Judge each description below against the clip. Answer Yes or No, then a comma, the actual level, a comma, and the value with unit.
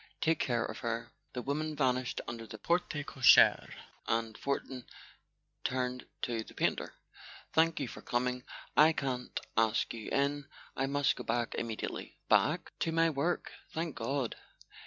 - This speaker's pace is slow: No, average, 145 wpm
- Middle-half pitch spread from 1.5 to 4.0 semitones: Yes, average, 3.7 semitones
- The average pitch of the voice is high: No, low, 130 Hz